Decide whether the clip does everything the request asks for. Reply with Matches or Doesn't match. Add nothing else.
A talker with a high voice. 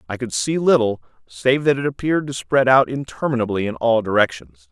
Doesn't match